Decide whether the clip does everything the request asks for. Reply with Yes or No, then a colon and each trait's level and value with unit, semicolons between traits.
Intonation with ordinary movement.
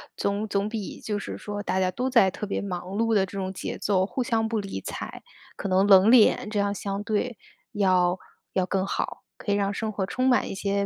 No: narrow, 2.1 semitones